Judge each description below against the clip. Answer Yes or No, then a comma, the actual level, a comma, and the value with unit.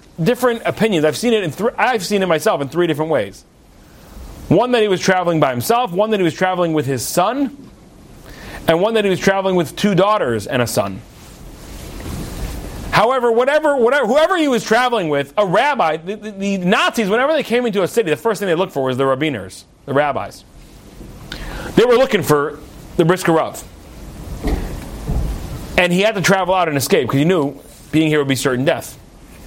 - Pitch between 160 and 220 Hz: Yes, medium, 185 Hz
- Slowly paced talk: No, average, 195 wpm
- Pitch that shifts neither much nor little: No, wide, 6.5 semitones